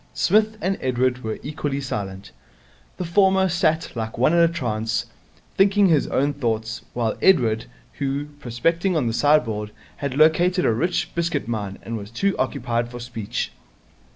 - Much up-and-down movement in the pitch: Yes, wide, 6.7 semitones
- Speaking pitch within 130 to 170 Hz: Yes, low, 135 Hz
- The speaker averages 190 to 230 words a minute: No, average, 155 wpm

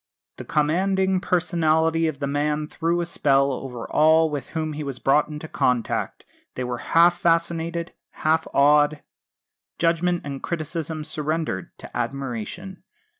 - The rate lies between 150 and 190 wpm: No, slow, 135 wpm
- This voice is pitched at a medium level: Yes, medium, 155 Hz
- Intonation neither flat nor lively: Yes, average, 3.0 semitones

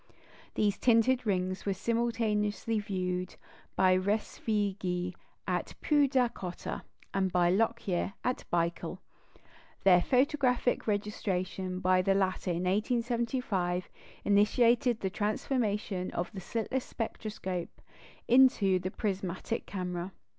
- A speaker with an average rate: No, slow, 100 wpm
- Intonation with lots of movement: No, average, 3.9 semitones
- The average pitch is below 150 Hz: No, high, 200 Hz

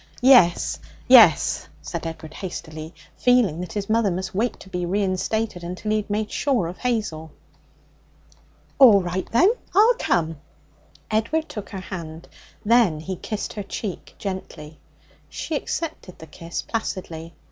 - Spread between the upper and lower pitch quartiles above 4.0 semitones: Yes, average, 4.7 semitones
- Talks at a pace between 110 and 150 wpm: Yes, average, 140 wpm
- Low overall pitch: No, high, 190 Hz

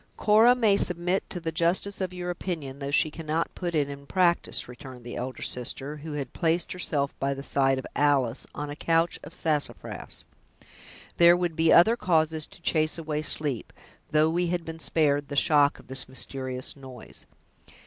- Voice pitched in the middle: Yes, medium, 155 Hz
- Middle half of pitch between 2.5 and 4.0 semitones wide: Yes, average, 3.6 semitones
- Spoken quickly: No, average, 180 wpm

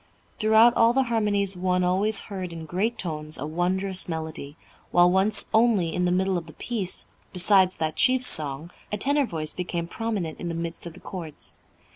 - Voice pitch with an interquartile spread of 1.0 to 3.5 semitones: No, average, 4.0 semitones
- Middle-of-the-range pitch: Yes, medium, 180 Hz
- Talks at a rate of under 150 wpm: No, average, 185 wpm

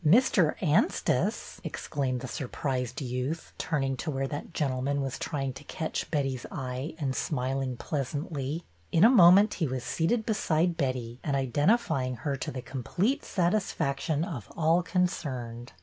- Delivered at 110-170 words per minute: Yes, average, 150 wpm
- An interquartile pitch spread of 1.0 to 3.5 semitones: No, average, 4.3 semitones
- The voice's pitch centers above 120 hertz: Yes, medium, 140 Hz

